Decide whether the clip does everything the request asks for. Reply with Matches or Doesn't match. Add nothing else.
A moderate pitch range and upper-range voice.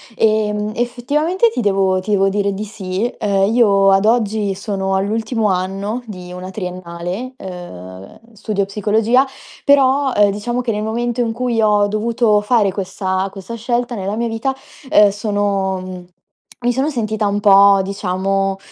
Matches